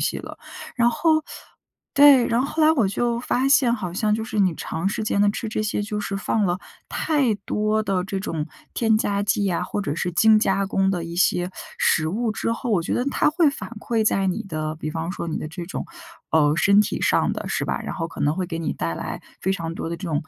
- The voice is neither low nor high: No, high, 200 Hz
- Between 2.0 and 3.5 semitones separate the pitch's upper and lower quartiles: No, average, 4.9 semitones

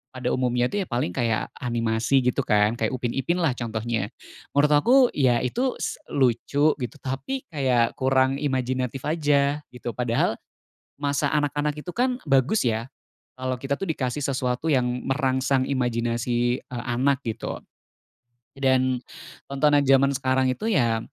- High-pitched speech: No, low, 130 Hz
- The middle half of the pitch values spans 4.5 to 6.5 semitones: No, average, 2.7 semitones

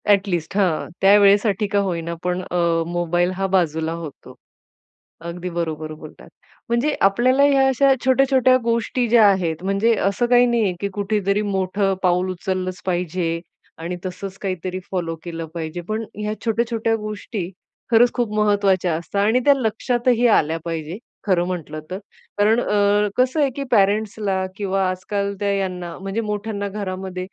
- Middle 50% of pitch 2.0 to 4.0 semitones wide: Yes, average, 3.5 semitones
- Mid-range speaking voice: No, high, 195 Hz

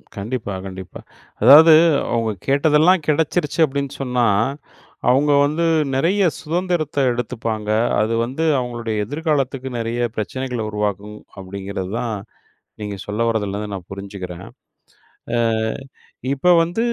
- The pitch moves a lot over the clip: Yes, wide, 5.9 semitones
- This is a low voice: Yes, low, 120 Hz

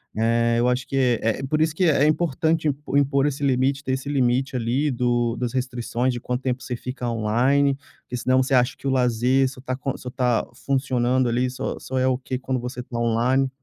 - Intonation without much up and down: Yes, narrow, 1.8 semitones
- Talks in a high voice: No, low, 130 Hz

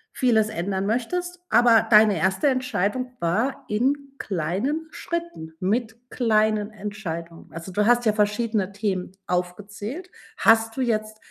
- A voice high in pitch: Yes, high, 215 Hz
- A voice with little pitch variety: No, average, 3.8 semitones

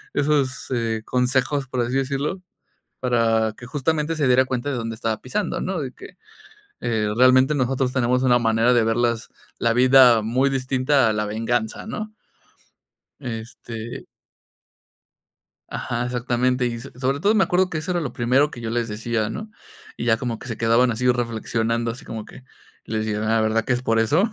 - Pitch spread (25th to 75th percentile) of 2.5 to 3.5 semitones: Yes, average, 2.8 semitones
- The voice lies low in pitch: Yes, low, 125 Hz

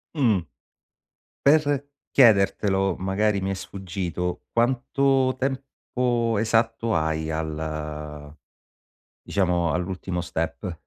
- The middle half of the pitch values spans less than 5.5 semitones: No, wide, 6.0 semitones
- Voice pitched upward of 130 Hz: No, very low, 95 Hz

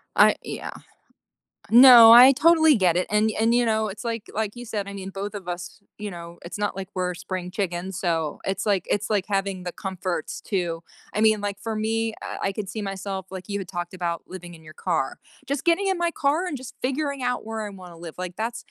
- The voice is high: Yes, high, 200 Hz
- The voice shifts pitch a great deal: No, average, 3.9 semitones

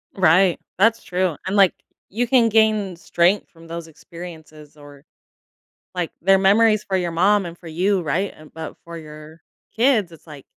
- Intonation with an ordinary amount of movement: Yes, average, 3.6 semitones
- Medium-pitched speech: Yes, medium, 180 Hz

